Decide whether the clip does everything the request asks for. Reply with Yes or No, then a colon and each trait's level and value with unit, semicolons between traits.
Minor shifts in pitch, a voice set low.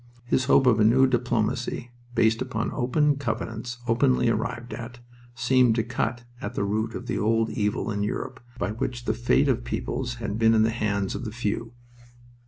Yes: narrow, 1.9 semitones; low, 115 Hz